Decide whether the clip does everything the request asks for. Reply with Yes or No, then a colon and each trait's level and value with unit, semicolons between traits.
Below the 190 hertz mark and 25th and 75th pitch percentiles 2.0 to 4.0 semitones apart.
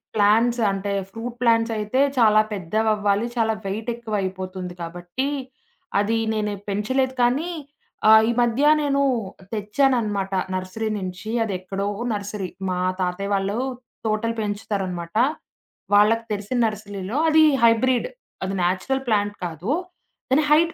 No: high, 210 Hz; average, 3.0 semitones